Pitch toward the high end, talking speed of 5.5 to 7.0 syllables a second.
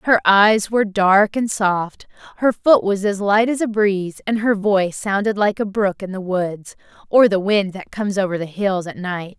No: high, 200 Hz; 4.7 syllables/s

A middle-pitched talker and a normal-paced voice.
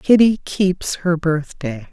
No: medium, 170 Hz; slow, 125 wpm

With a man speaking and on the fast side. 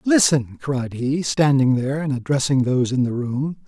No: male; average, 180 wpm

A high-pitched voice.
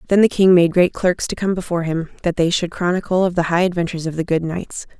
No: medium, 175 Hz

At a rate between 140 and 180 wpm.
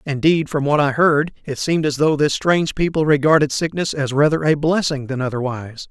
No: fast, 205 wpm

